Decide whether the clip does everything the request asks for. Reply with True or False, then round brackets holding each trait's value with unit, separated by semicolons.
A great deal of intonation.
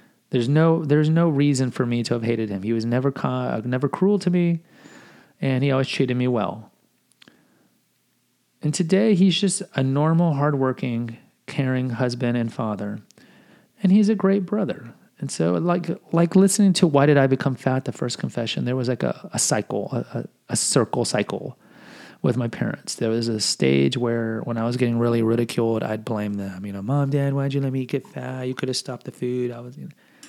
True (5.9 semitones)